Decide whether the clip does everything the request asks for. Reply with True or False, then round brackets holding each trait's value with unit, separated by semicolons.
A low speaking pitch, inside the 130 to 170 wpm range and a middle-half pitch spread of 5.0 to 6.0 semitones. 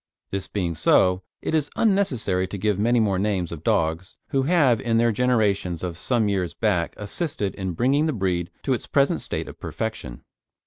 False (105 Hz; 185 wpm; 5.4 semitones)